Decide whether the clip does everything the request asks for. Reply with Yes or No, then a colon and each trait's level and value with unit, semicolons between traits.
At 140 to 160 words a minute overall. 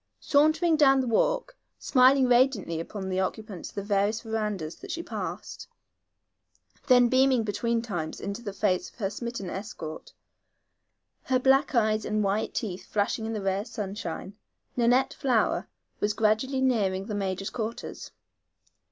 Yes: average, 145 wpm